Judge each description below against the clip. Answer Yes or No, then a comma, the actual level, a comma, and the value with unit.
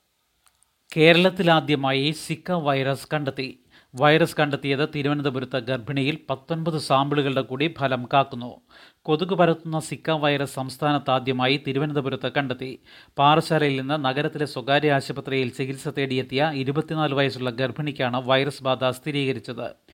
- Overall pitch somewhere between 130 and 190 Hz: Yes, medium, 140 Hz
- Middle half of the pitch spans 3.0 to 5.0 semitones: No, narrow, 2.4 semitones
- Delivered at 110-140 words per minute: No, average, 100 wpm